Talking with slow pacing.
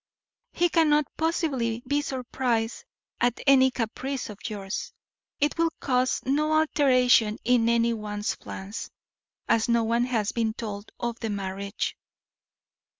Yes: slow, 130 wpm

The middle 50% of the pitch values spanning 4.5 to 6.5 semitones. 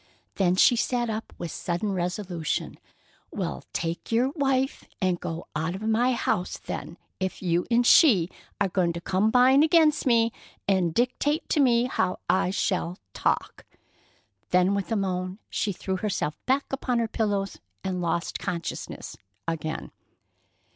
Yes: average, 5.2 semitones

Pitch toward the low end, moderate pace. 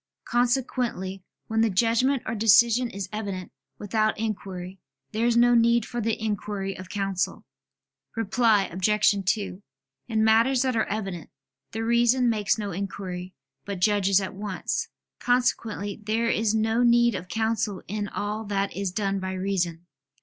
No: high, 210 Hz; average, 150 wpm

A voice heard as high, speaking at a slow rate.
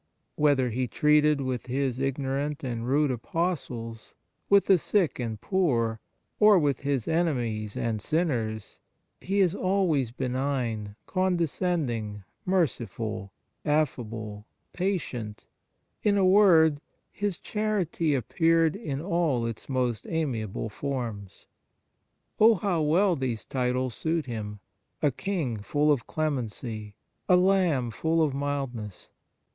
No: medium, 140 Hz; slow, 115 wpm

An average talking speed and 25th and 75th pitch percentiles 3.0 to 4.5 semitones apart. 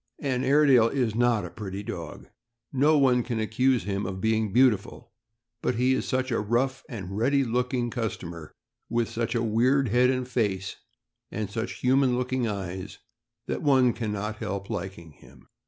Yes: average, 175 wpm; average, 3.7 semitones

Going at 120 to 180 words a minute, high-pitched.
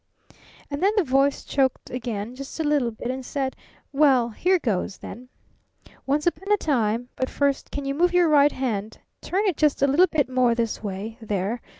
No: average, 195 wpm; very high, 270 Hz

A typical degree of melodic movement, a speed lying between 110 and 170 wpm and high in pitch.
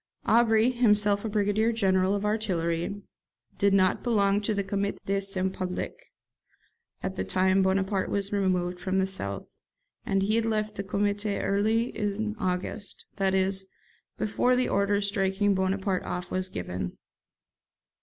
No: narrow, 1.7 semitones; average, 145 wpm; high, 200 Hz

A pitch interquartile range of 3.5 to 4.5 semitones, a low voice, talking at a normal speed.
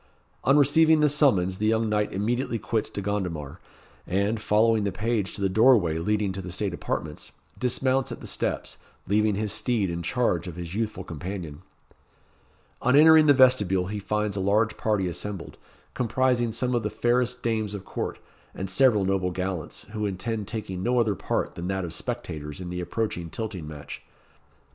Yes: average, 4.2 semitones; low, 105 Hz; average, 175 wpm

